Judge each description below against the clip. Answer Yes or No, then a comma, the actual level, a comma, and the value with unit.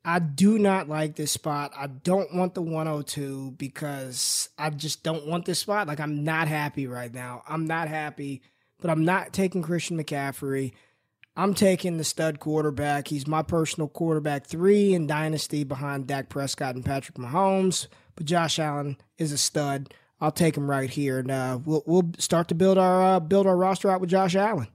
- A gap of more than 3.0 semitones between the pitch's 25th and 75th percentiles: Yes, average, 3.8 semitones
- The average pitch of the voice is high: No, medium, 155 Hz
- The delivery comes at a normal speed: Yes, average, 190 wpm